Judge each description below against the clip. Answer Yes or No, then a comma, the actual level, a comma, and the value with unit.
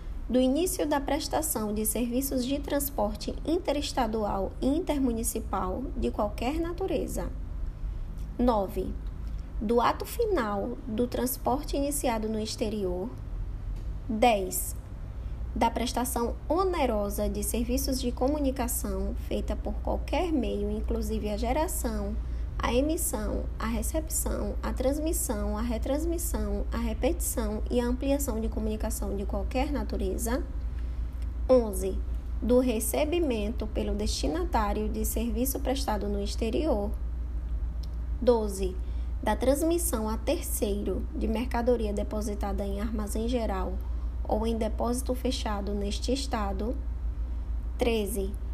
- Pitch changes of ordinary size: Yes, average, 4.6 semitones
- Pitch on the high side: Yes, high, 225 Hz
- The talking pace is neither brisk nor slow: No, slow, 105 wpm